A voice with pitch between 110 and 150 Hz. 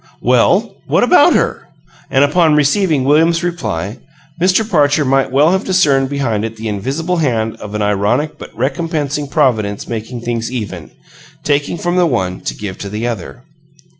Yes: low, 135 Hz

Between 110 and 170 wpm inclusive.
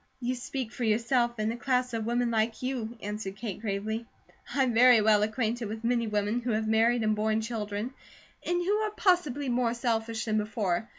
No: average, 190 wpm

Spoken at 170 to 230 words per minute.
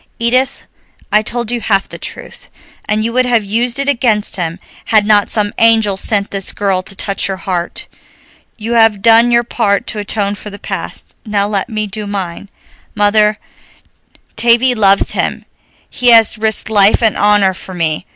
Yes: average, 175 wpm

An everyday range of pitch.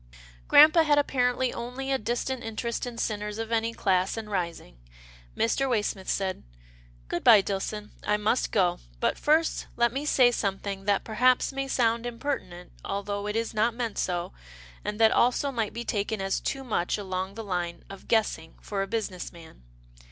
Yes: average, 3.9 semitones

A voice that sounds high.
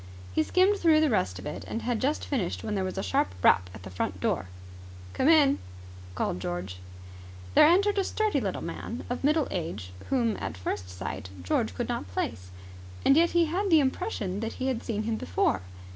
Yes: high, 225 Hz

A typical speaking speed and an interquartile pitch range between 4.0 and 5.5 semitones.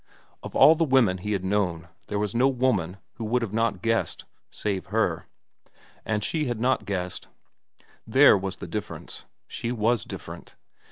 Yes: average, 160 wpm; average, 4.3 semitones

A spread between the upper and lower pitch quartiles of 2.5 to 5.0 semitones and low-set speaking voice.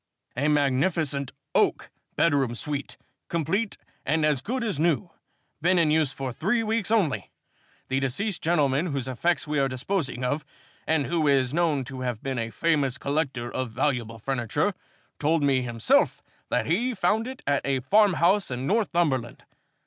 No: average, 4.7 semitones; medium, 145 Hz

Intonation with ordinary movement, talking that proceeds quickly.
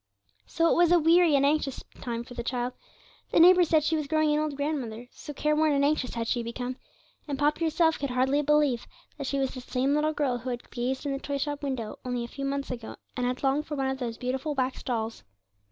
Yes: average, 3.2 semitones; fast, 240 wpm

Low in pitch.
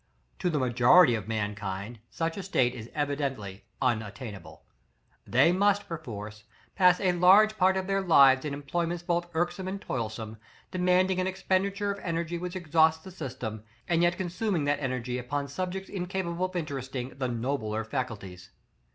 No: medium, 155 Hz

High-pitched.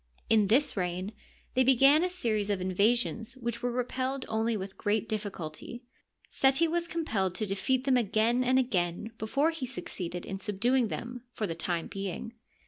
Yes: high, 225 Hz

